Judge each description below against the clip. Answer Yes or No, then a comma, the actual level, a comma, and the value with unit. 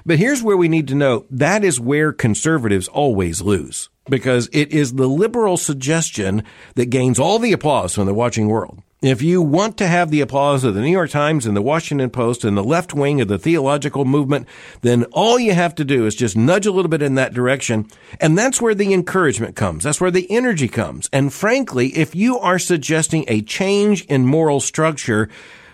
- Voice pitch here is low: No, medium, 145 Hz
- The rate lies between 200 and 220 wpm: Yes, fast, 205 wpm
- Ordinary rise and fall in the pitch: No, wide, 6.0 semitones